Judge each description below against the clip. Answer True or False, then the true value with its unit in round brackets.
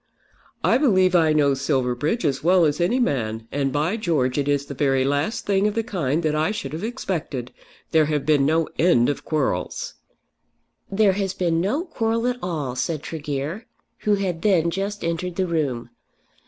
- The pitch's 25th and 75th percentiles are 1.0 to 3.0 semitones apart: False (5.3 semitones)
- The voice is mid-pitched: True (160 Hz)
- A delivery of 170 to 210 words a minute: True (180 wpm)